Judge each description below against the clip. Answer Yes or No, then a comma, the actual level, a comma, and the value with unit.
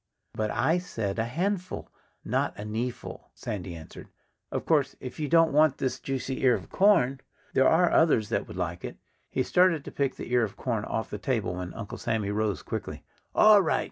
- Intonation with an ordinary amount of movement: No, wide, 7.0 semitones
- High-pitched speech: No, low, 125 Hz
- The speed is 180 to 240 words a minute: Yes, average, 200 wpm